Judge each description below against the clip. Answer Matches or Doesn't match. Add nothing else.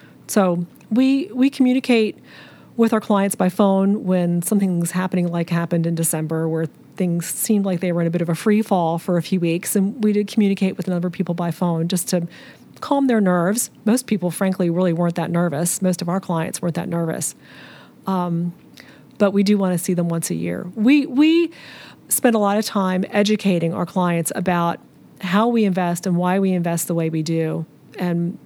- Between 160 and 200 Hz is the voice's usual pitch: Matches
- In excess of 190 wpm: Matches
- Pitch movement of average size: Matches